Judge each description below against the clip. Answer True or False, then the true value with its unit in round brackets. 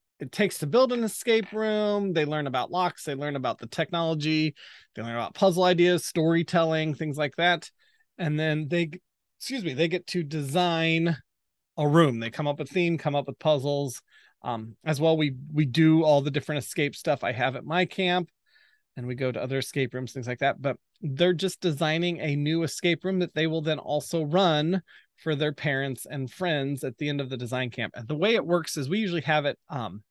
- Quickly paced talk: True (215 wpm)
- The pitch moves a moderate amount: True (3.7 semitones)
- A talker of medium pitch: True (155 Hz)